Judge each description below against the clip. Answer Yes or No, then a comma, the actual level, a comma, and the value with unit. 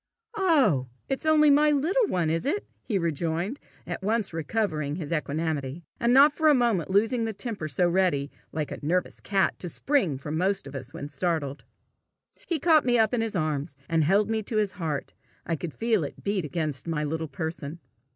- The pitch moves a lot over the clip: Yes, wide, 7.1 semitones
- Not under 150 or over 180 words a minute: No, average, 190 wpm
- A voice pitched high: No, medium, 180 Hz